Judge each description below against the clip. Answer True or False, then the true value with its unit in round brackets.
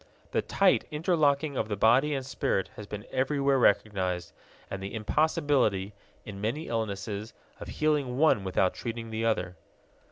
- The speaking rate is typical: True (150 wpm)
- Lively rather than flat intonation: True (5.8 semitones)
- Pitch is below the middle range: True (115 Hz)